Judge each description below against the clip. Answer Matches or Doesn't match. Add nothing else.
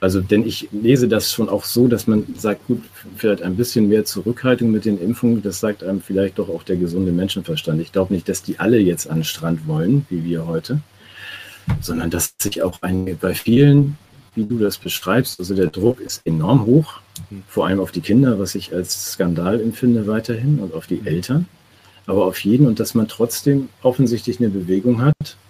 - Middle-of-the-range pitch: Doesn't match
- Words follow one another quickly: Matches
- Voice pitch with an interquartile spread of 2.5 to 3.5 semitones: Doesn't match